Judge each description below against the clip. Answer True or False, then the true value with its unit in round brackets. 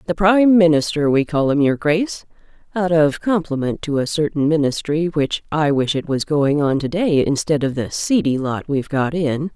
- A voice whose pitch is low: False (155 Hz)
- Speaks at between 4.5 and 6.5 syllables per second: True (5.0 syllables/s)